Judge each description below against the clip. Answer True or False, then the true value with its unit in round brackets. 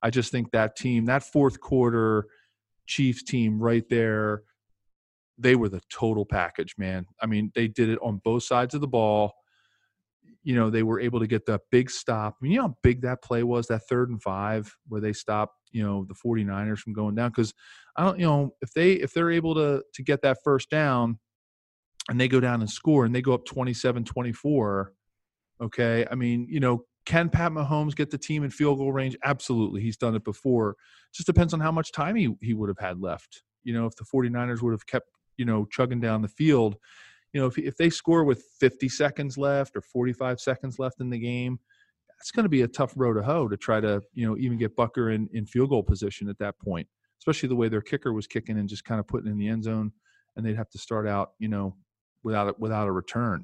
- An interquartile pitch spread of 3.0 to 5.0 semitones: True (3.7 semitones)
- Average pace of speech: False (230 wpm)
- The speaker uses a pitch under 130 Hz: True (120 Hz)